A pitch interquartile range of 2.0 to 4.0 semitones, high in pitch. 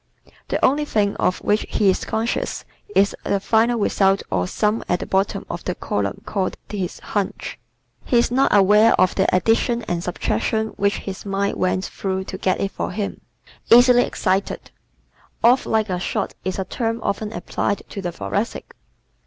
Yes: average, 2.8 semitones; high, 200 Hz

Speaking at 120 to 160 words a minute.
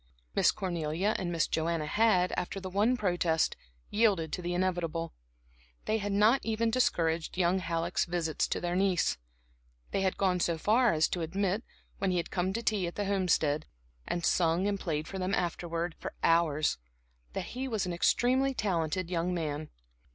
No: average, 175 wpm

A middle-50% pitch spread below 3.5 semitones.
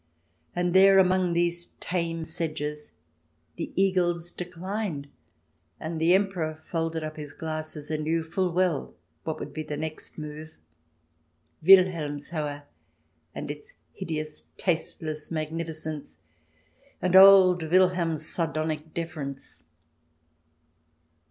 Yes: narrow, 2.5 semitones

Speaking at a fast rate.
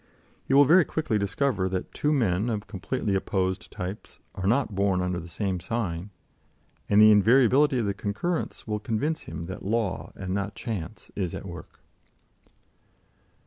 No: average, 160 wpm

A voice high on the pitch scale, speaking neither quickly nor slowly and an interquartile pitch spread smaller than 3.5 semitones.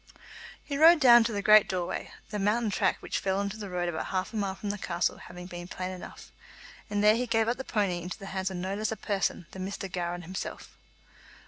No: high, 195 Hz; fast, 240 wpm; average, 2.9 semitones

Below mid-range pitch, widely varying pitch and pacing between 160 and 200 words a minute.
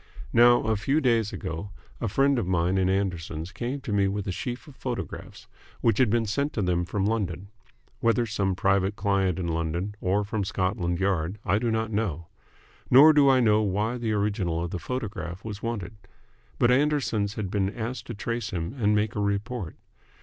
No: low, 105 Hz; average, 3.8 semitones; average, 195 wpm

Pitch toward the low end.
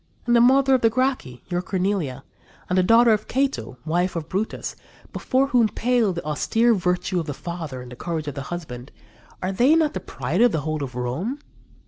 No: medium, 180 Hz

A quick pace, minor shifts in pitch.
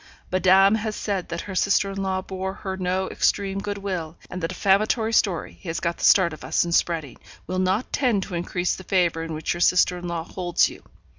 Yes: fast, 225 wpm; narrow, 2.3 semitones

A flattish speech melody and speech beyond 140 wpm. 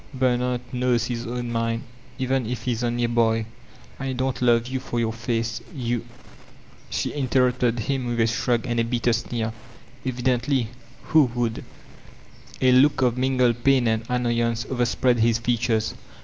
Yes: narrow, 1.5 semitones; average, 175 wpm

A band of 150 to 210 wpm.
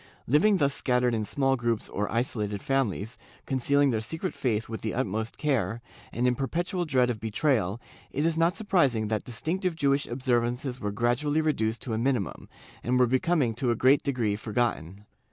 Yes: average, 180 wpm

